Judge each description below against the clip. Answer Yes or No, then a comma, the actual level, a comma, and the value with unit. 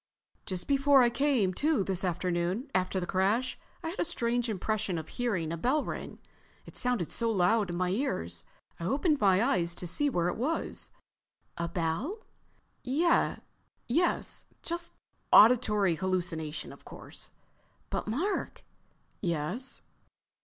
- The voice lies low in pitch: No, high, 210 Hz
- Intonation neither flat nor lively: No, wide, 7.0 semitones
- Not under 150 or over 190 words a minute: No, slow, 135 wpm